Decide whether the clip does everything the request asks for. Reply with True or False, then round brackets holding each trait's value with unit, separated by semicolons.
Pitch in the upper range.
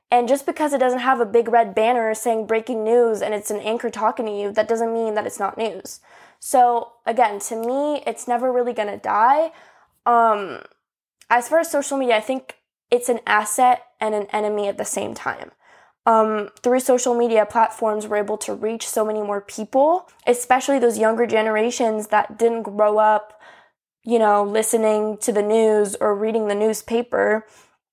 True (225 Hz)